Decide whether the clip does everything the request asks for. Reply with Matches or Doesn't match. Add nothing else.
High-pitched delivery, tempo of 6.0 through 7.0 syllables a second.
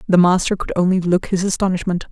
Doesn't match